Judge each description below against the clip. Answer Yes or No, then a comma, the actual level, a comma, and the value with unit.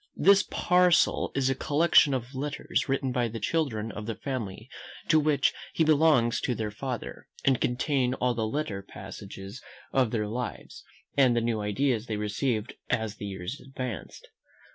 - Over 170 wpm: No, average, 165 wpm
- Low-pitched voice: Yes, low, 125 Hz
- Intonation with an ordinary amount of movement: Yes, average, 4.3 semitones